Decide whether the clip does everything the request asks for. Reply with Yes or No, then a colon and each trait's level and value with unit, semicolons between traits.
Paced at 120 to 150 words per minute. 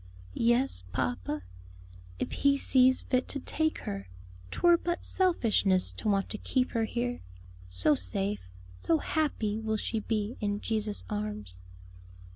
Yes: slow, 135 wpm